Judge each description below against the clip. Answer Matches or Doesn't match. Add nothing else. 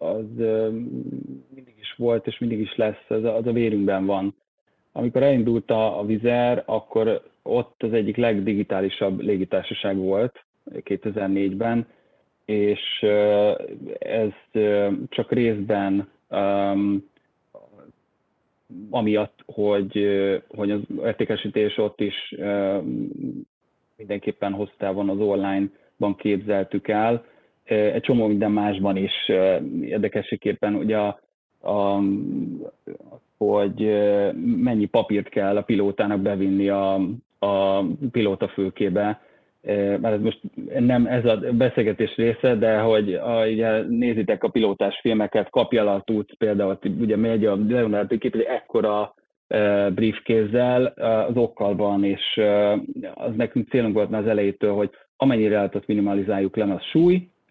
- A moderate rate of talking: Matches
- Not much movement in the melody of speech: Matches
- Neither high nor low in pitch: Doesn't match